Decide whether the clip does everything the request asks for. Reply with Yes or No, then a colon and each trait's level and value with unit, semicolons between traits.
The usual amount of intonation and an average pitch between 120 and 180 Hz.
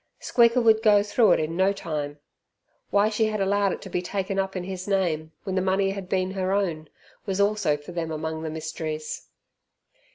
No: average, 4.0 semitones; high, 190 Hz